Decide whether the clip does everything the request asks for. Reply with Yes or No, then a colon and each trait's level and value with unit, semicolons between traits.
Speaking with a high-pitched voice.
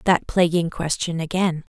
No: medium, 170 Hz